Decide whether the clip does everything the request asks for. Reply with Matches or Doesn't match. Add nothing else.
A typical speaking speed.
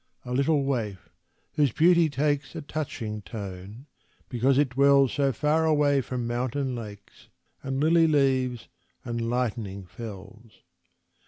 Doesn't match